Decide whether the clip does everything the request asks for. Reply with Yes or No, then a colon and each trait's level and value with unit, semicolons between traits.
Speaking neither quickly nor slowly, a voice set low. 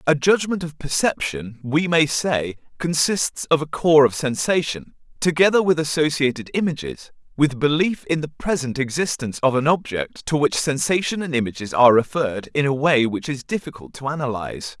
No: average, 165 wpm; medium, 145 Hz